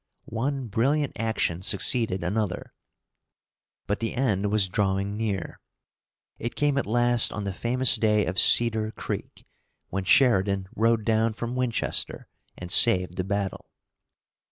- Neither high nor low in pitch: No, low, 110 Hz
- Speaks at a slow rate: Yes, slow, 130 wpm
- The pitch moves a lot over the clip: No, average, 3.4 semitones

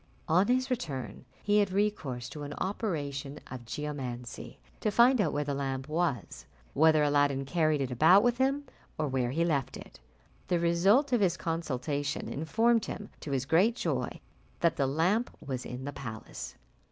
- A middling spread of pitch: No, wide, 6.5 semitones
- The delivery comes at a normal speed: Yes, average, 170 wpm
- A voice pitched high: No, medium, 155 Hz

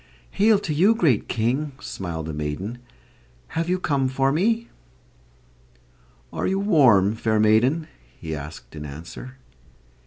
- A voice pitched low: Yes, low, 130 Hz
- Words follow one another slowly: Yes, slow, 130 wpm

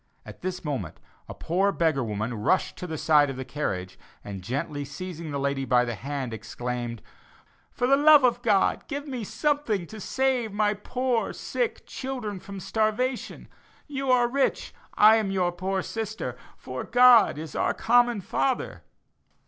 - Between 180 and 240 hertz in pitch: Yes, high, 190 Hz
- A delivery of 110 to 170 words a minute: Yes, average, 165 wpm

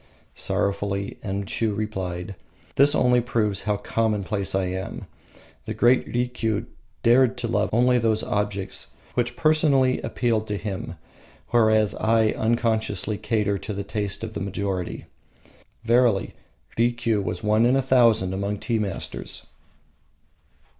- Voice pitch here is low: Yes, low, 110 Hz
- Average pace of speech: No, slow, 125 wpm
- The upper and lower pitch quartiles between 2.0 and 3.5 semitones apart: Yes, average, 3.0 semitones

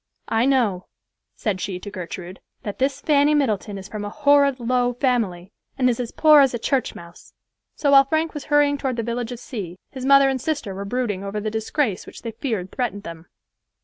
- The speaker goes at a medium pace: No, fast, 210 wpm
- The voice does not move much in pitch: No, average, 5.3 semitones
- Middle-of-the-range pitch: No, high, 240 Hz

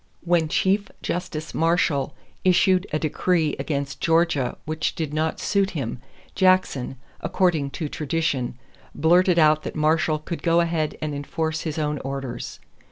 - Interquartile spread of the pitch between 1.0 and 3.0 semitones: Yes, narrow, 2.6 semitones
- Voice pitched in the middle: Yes, medium, 160 Hz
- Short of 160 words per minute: Yes, average, 140 wpm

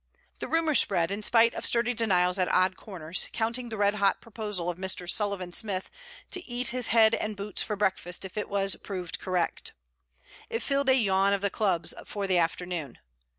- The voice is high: Yes, high, 200 Hz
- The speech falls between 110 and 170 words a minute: No, average, 195 wpm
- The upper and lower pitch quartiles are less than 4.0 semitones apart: Yes, average, 3.6 semitones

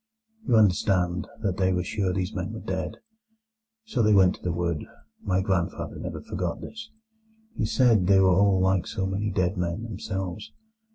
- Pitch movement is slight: Yes, narrow, 2.3 semitones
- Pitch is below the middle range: Yes, very low, 95 Hz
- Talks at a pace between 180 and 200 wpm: No, average, 170 wpm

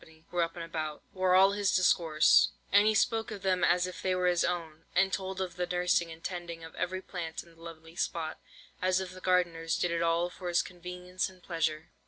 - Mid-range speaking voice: Yes, medium, 180 Hz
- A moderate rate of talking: No, fast, 225 wpm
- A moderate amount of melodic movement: No, narrow, 1.8 semitones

